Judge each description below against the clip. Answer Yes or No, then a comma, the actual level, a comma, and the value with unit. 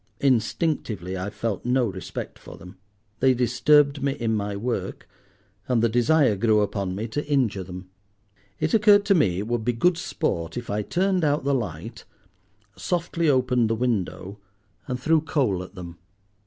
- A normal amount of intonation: No, wide, 6.2 semitones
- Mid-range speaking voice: No, low, 120 Hz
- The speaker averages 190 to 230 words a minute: No, average, 170 wpm